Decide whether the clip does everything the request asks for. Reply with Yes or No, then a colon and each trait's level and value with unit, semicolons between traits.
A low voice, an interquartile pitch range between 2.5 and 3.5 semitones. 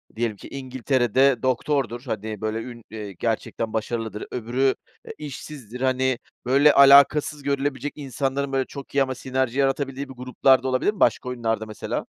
Yes: low, 130 Hz; average, 2.8 semitones